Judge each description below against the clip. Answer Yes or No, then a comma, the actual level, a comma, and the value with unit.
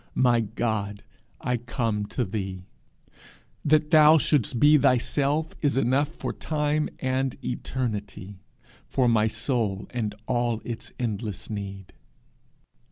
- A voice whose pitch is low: Yes, low, 120 Hz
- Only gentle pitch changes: No, average, 4.8 semitones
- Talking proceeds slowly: Yes, slow, 115 wpm